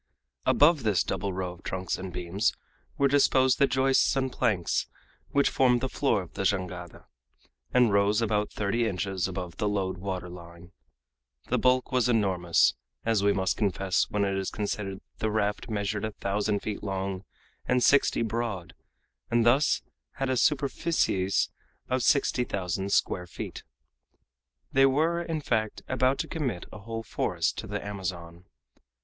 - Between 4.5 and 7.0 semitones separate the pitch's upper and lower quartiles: Yes, average, 5.0 semitones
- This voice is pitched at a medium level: No, low, 105 Hz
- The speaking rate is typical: Yes, average, 160 wpm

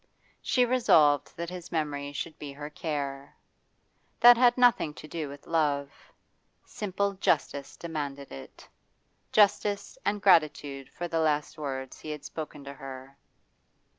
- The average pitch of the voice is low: No, medium, 150 Hz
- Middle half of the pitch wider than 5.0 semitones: No, average, 4.2 semitones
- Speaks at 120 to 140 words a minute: Yes, slow, 135 wpm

